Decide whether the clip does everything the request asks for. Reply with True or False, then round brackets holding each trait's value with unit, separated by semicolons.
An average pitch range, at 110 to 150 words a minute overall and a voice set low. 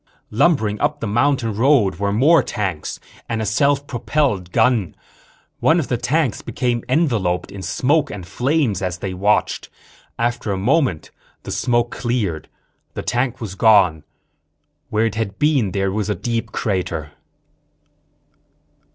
True (4.8 semitones; 140 wpm; 115 Hz)